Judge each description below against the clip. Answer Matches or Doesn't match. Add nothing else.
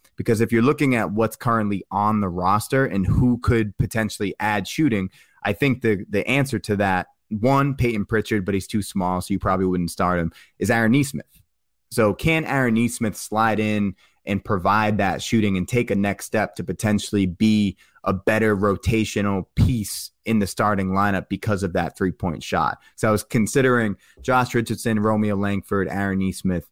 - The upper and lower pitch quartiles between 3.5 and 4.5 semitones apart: Doesn't match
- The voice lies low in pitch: Matches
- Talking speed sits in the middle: Matches